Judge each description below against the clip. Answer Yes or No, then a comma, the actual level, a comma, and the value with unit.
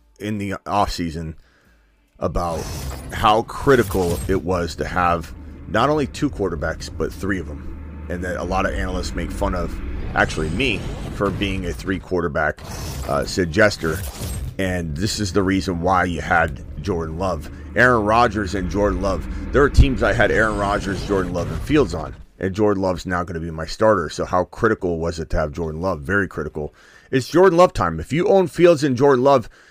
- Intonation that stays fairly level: No, average, 3.7 semitones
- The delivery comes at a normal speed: Yes, average, 190 wpm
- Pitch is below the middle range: Yes, very low, 90 Hz